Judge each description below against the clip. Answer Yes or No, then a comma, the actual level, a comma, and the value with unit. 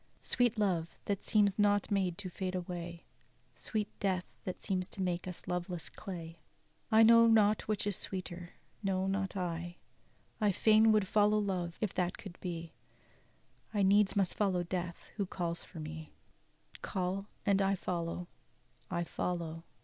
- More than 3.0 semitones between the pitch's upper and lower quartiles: No, average, 2.7 semitones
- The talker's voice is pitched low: No, medium, 185 Hz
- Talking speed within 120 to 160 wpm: Yes, average, 155 wpm